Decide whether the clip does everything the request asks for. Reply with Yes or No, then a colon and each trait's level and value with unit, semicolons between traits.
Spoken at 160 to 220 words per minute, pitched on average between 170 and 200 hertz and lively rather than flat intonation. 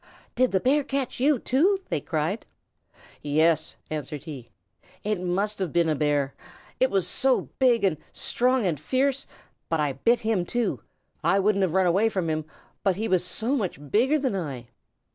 Yes: average, 180 wpm; high, 190 Hz; wide, 7.5 semitones